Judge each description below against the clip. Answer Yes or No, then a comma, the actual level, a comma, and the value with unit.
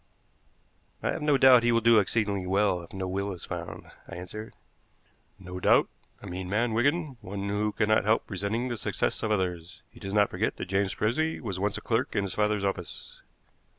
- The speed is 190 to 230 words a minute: Yes, average, 200 wpm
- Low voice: Yes, low, 100 Hz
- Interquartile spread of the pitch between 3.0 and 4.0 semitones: Yes, average, 3.3 semitones